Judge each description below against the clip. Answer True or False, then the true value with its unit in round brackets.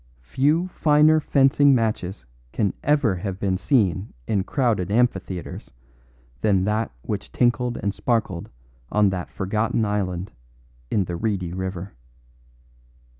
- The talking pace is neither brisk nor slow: False (120 wpm)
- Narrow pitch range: False (4.7 semitones)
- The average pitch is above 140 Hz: False (105 Hz)